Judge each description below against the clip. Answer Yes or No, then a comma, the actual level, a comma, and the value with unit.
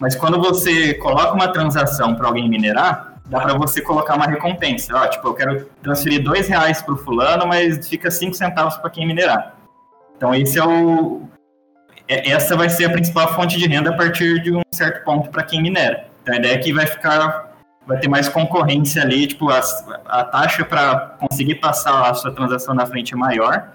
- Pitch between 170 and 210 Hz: No, medium, 155 Hz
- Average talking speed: No, fast, 200 wpm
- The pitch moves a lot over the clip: No, average, 4.0 semitones